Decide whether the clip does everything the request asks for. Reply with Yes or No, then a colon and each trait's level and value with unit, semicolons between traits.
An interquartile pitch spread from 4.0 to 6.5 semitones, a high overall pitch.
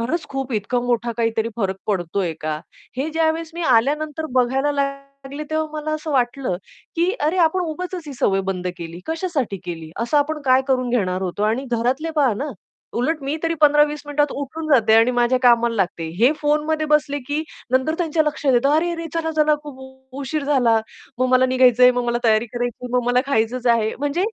Yes: average, 4.3 semitones; very high, 265 Hz